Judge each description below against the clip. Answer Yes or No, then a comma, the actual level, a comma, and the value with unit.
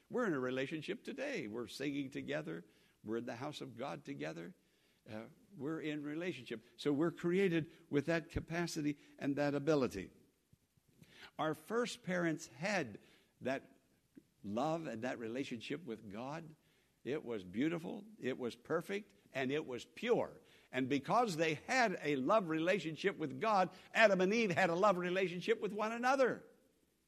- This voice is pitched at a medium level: Yes, medium, 160 Hz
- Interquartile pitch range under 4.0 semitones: No, average, 5.1 semitones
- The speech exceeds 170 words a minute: No, average, 150 wpm